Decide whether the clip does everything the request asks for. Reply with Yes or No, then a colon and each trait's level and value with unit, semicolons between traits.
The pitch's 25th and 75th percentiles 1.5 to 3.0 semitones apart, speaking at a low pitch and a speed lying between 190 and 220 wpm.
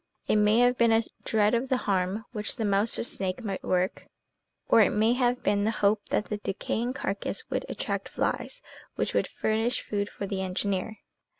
No: narrow, 2.5 semitones; high, 210 Hz; average, 195 wpm